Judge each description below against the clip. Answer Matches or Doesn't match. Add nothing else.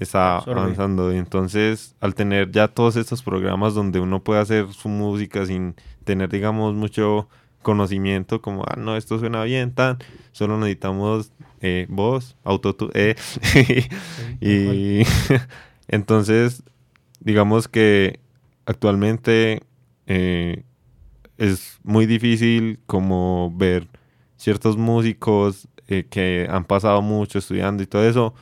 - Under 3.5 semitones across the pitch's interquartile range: Matches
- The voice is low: Matches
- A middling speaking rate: Doesn't match